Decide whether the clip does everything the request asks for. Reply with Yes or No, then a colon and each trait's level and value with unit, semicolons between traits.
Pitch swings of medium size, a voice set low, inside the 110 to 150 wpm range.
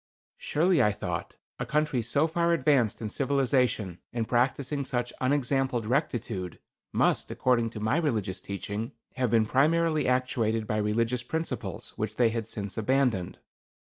Yes: average, 4.3 semitones; low, 125 Hz; average, 140 wpm